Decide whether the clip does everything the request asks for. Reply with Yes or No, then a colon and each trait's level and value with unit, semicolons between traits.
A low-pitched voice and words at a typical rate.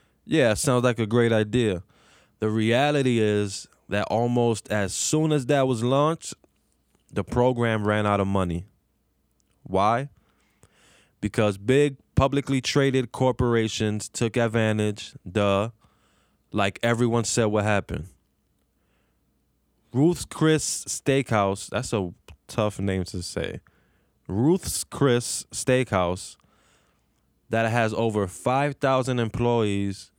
No: low, 110 Hz; slow, 105 wpm